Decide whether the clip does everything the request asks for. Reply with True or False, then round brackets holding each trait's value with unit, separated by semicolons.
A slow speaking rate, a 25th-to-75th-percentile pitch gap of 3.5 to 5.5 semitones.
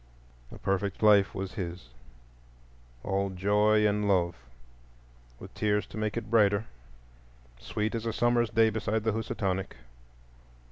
False (125 wpm; 2.7 semitones)